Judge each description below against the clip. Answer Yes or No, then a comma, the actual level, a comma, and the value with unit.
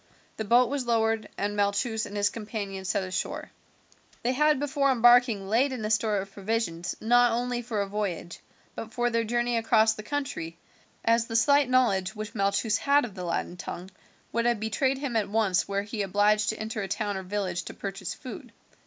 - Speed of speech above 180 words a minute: Yes, average, 200 wpm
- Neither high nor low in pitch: No, high, 220 Hz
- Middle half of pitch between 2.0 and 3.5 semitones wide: Yes, average, 3.2 semitones